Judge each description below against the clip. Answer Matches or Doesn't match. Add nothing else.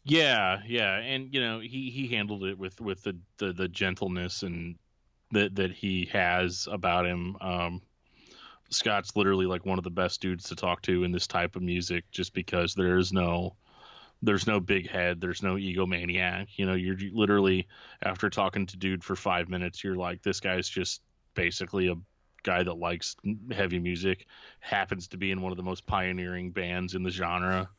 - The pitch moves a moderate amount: Doesn't match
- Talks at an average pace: Matches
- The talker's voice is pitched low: Matches